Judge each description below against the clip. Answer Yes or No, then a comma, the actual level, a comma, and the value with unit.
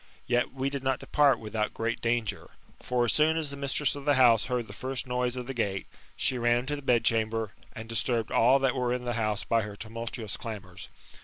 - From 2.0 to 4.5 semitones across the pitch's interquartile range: Yes, average, 2.9 semitones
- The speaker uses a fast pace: Yes, fast, 220 wpm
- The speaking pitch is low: Yes, low, 120 Hz